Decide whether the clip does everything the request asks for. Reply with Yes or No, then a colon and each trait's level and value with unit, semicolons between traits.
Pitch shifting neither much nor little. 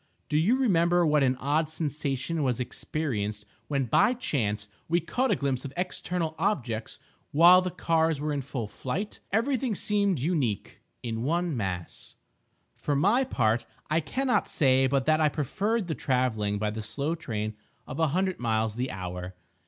No: wide, 6.6 semitones